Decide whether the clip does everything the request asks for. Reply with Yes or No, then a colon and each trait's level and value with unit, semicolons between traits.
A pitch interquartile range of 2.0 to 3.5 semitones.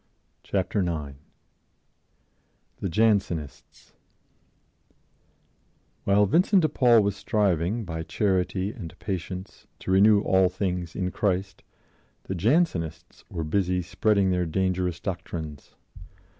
Yes: average, 2.9 semitones